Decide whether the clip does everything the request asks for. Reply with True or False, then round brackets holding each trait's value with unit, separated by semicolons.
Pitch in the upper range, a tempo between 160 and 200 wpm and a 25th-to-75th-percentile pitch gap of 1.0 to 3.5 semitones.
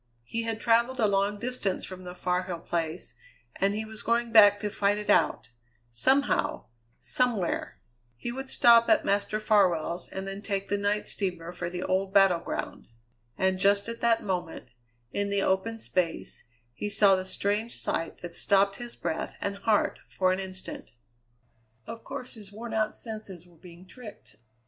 True (200 Hz; 170 wpm; 3.1 semitones)